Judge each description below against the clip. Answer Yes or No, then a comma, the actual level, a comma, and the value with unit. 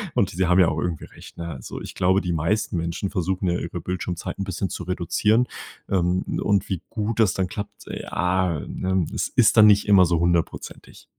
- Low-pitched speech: Yes, very low, 90 Hz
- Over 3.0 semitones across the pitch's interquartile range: No, narrow, 2.5 semitones